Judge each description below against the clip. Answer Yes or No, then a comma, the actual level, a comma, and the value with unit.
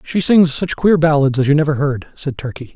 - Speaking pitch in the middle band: Yes, medium, 150 Hz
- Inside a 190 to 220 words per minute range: No, fast, 240 wpm